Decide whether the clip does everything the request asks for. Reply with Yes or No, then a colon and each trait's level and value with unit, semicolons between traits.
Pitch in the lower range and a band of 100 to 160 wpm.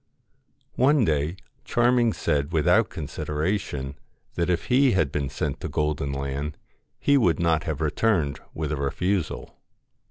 Yes: very low, 80 Hz; slow, 135 wpm